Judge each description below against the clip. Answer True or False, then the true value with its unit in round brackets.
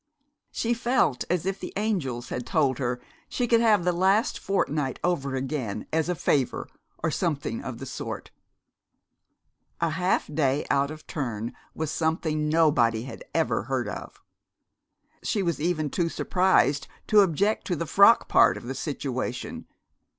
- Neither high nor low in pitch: True (160 Hz)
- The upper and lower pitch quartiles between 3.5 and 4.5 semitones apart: False (5.5 semitones)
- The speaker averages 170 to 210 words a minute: False (155 wpm)